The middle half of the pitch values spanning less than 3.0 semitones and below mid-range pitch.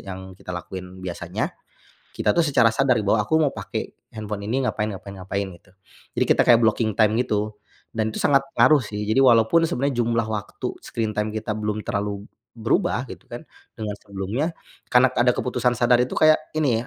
No: average, 3.3 semitones; low, 110 Hz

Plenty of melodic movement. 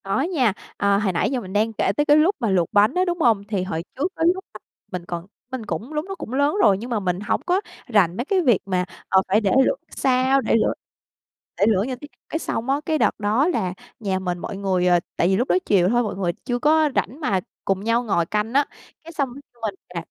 Yes: wide, 6.5 semitones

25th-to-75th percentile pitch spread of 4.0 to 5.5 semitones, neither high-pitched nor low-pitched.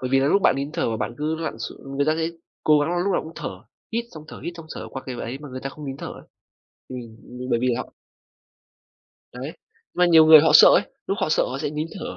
No: average, 3.4 semitones; medium, 150 Hz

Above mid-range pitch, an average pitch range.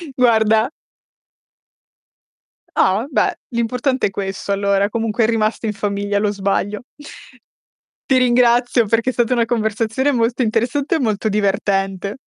Yes: high, 220 Hz; average, 3.0 semitones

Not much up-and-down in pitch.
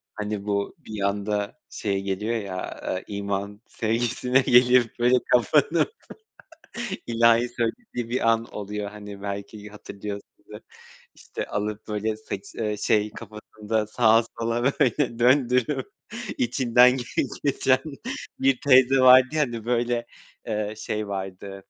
No: average, 3.1 semitones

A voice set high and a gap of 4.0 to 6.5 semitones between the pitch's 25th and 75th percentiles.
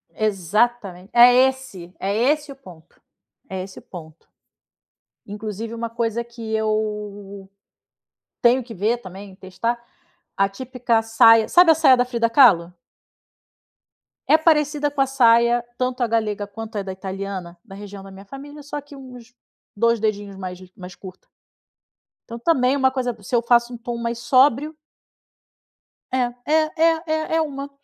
Yes: high, 230 Hz; average, 4.5 semitones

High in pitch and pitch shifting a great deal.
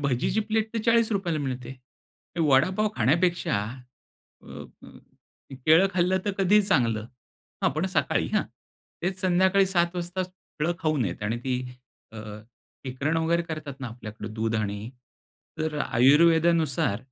No: medium, 160 Hz; wide, 6.5 semitones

